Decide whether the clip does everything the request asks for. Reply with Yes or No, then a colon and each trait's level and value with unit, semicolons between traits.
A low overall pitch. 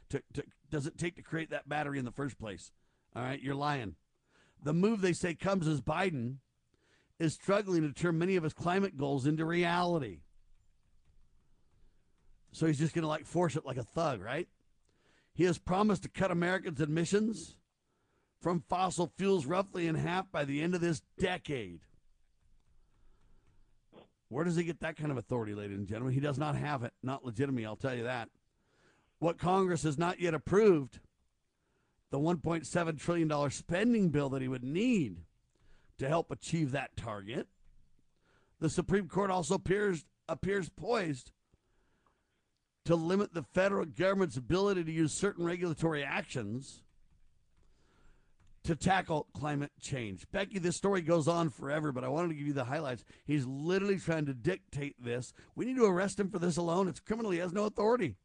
No: medium, 160 Hz